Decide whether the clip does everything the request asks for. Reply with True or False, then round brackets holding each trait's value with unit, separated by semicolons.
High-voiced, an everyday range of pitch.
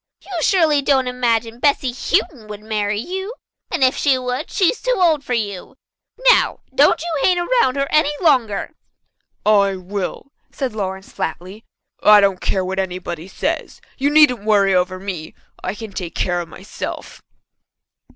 False (225 Hz; 6.7 semitones)